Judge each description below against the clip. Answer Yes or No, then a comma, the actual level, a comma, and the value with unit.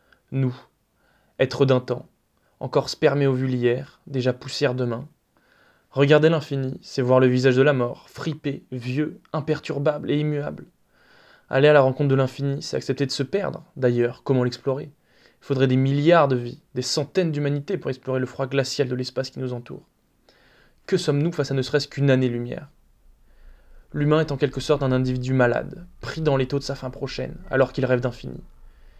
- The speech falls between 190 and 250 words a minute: No, average, 180 wpm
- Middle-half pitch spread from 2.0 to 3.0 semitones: Yes, narrow, 2.5 semitones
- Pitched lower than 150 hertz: Yes, low, 135 Hz